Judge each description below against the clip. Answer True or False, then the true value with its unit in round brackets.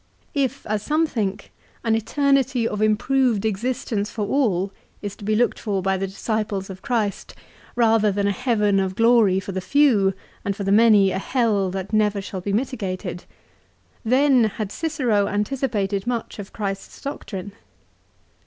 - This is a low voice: False (210 Hz)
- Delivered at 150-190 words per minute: True (160 wpm)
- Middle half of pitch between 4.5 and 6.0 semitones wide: False (3.7 semitones)